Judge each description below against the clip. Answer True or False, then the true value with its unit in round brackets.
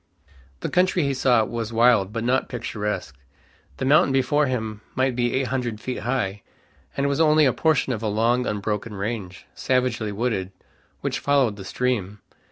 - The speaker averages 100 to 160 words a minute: False (170 wpm)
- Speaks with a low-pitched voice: True (120 Hz)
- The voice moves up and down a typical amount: True (3.8 semitones)